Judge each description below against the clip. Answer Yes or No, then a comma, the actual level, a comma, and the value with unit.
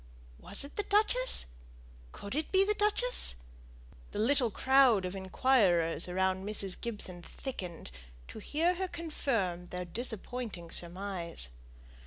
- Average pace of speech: No, slow, 125 wpm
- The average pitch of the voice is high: Yes, high, 210 Hz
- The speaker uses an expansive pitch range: Yes, wide, 8.1 semitones